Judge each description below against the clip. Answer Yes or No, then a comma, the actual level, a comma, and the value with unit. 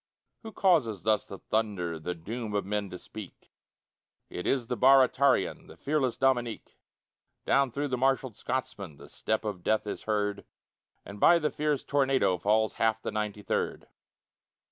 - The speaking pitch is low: Yes, low, 110 Hz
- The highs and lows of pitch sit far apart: No, average, 4.5 semitones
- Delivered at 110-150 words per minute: No, average, 160 wpm